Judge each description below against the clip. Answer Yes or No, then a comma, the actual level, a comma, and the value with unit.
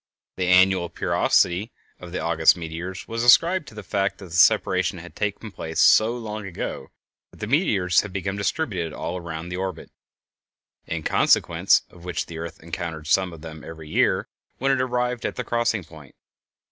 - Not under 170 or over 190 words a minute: Yes, average, 180 wpm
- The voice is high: No, very low, 90 Hz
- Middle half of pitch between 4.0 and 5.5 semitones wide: Yes, average, 4.4 semitones